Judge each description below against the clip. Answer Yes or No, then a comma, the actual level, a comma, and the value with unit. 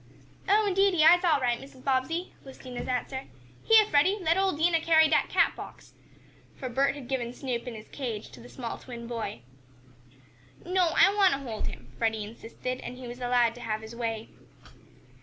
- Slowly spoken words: No, average, 190 wpm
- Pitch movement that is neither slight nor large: No, wide, 5.7 semitones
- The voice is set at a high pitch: Yes, very high, 260 Hz